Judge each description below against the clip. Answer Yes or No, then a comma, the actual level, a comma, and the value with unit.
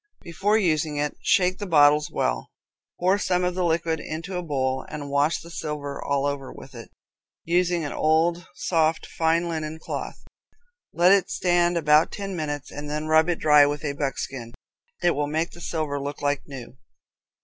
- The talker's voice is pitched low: No, medium, 155 Hz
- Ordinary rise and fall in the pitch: Yes, average, 3.0 semitones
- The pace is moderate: Yes, average, 180 wpm